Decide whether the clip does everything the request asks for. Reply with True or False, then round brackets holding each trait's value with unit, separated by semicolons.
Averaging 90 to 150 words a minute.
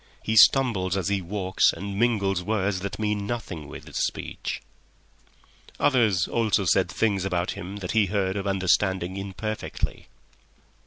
True (145 wpm)